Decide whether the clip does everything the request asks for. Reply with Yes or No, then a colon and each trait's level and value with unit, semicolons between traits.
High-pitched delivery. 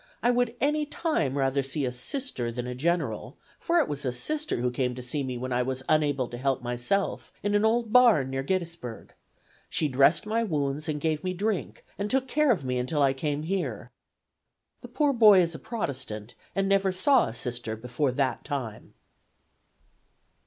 No: medium, 145 Hz